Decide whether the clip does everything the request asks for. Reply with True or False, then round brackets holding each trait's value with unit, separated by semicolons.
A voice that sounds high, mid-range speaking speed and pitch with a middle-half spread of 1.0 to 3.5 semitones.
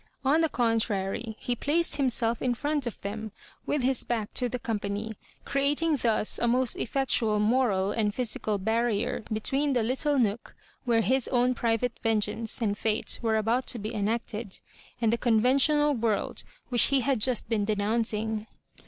True (230 Hz; 170 wpm; 2.9 semitones)